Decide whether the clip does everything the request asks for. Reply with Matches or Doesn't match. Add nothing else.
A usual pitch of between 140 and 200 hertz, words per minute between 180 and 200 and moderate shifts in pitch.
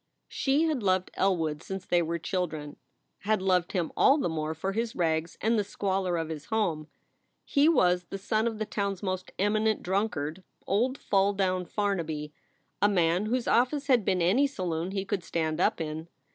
Matches